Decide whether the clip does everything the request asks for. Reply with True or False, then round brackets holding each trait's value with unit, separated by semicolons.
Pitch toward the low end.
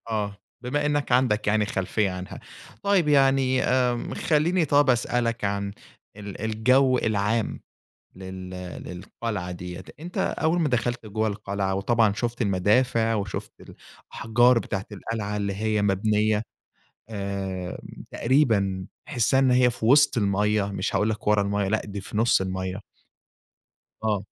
True (110 Hz)